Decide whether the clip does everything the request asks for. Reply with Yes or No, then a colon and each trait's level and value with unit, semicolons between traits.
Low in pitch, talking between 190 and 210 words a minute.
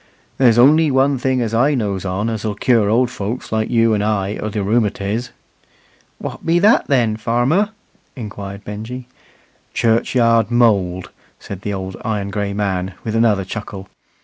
No: low, 110 Hz; average, 155 wpm